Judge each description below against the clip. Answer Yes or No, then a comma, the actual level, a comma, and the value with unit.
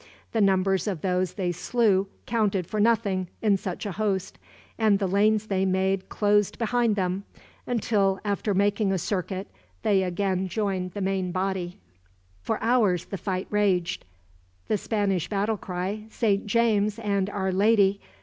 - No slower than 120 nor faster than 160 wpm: Yes, average, 150 wpm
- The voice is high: Yes, high, 195 Hz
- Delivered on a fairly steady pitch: Yes, narrow, 1.9 semitones